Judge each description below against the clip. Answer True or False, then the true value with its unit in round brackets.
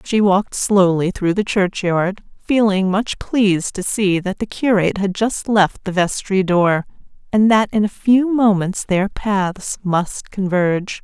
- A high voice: True (195 Hz)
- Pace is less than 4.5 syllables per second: True (4.0 syllables/s)